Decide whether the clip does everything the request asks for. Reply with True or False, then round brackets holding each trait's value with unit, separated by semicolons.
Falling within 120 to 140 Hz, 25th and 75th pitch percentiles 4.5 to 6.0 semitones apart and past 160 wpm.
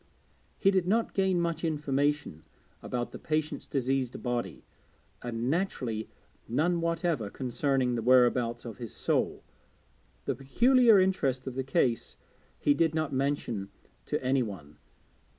False (135 Hz; 5.3 semitones; 135 wpm)